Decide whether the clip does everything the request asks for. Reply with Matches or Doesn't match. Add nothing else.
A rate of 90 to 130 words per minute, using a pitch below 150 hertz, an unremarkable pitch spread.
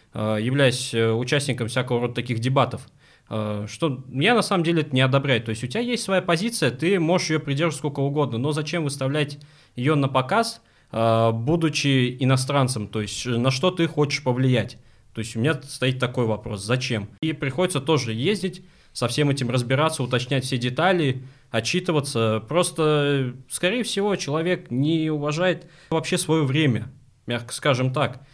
Doesn't match